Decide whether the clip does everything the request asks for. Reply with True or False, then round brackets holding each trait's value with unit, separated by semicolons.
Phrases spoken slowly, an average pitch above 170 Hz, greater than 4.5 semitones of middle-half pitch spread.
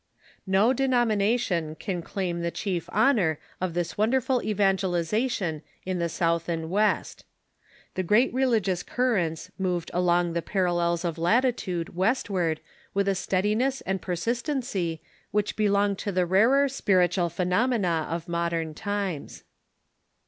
False (125 wpm; 190 Hz; 4.0 semitones)